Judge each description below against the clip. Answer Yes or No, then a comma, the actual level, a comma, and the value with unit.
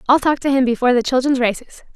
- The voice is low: No, very high, 260 Hz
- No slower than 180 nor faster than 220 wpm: No, fast, 245 wpm